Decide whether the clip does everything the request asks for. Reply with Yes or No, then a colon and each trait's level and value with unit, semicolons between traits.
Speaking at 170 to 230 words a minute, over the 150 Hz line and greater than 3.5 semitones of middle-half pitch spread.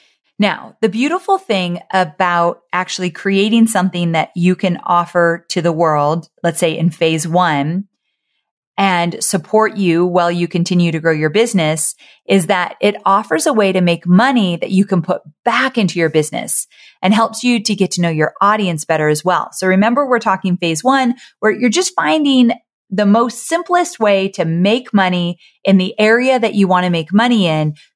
Yes: average, 180 wpm; medium, 185 Hz; average, 4.2 semitones